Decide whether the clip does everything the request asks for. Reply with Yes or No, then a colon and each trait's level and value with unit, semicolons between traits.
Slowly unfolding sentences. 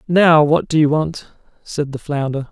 No: average, 190 wpm